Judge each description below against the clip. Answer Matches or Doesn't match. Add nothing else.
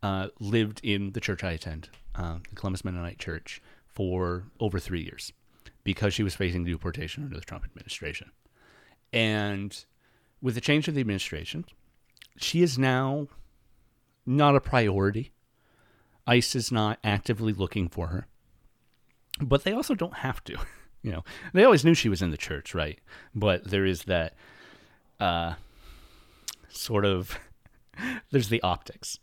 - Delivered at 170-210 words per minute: Doesn't match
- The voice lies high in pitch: Doesn't match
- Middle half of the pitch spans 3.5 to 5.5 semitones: Matches